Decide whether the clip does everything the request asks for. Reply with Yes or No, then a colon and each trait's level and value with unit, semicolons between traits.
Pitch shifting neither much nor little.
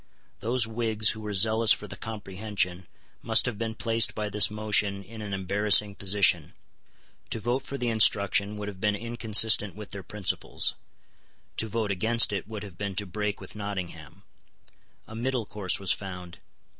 No: narrow, 2.0 semitones